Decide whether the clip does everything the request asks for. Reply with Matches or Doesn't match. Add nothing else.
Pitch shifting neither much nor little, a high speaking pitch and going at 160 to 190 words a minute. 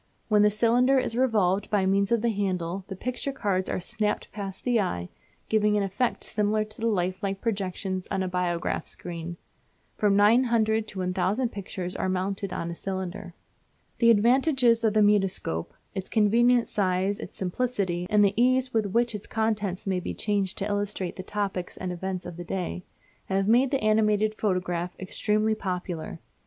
Matches